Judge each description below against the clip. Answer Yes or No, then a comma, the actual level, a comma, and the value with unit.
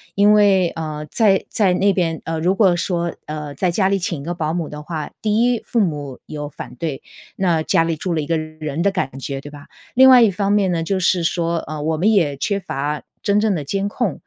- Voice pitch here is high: No, medium, 170 Hz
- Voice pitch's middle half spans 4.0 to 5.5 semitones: Yes, average, 4.4 semitones